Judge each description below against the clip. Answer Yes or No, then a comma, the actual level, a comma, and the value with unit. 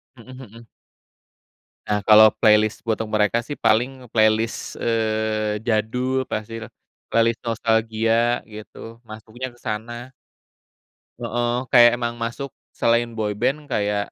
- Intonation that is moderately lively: No, narrow, 1.6 semitones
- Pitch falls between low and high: No, low, 115 Hz